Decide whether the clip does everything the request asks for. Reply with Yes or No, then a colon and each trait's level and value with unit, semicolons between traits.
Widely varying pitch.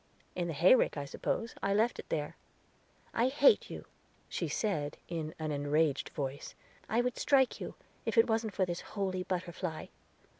Yes: wide, 6.5 semitones